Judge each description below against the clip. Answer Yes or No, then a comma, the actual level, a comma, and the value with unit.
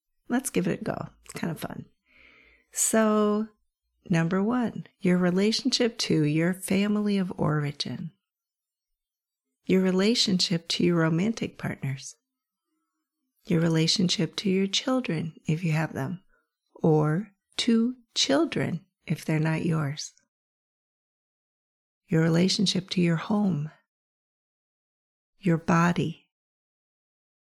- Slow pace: Yes, slow, 105 wpm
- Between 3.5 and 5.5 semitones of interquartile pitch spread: Yes, average, 4.8 semitones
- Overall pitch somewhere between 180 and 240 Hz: Yes, medium, 185 Hz